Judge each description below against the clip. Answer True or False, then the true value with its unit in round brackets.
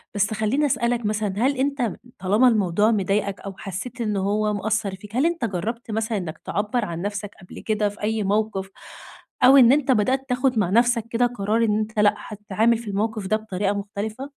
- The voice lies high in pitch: True (215 Hz)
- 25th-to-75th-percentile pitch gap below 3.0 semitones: True (2.6 semitones)